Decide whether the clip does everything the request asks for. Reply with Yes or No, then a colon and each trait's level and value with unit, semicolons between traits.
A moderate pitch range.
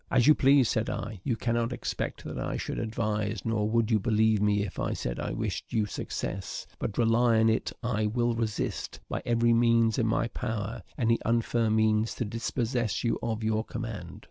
No: narrow, 1.4 semitones